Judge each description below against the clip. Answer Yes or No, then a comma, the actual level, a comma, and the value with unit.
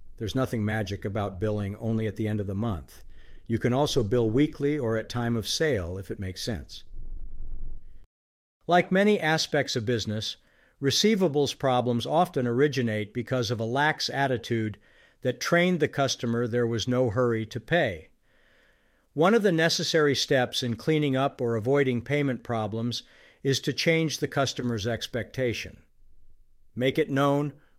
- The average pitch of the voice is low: Yes, low, 120 Hz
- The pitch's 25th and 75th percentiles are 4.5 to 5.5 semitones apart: Yes, average, 4.8 semitones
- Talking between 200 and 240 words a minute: No, average, 155 wpm